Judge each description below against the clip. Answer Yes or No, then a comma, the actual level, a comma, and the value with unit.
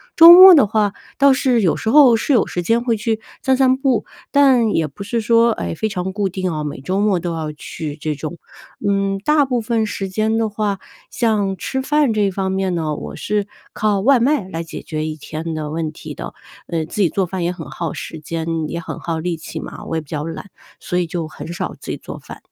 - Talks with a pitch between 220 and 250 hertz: No, high, 195 Hz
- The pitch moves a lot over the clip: Yes, wide, 5.8 semitones